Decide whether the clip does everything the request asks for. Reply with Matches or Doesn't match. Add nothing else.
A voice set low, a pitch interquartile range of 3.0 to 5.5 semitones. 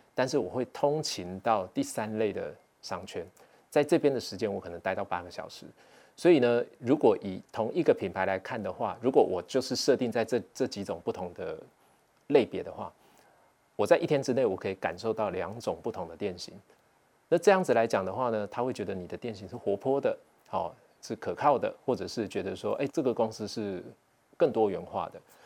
Matches